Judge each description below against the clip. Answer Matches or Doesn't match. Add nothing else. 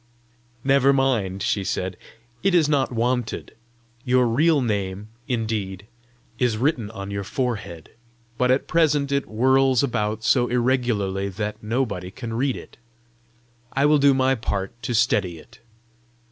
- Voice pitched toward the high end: Doesn't match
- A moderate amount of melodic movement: Matches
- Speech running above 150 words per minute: Doesn't match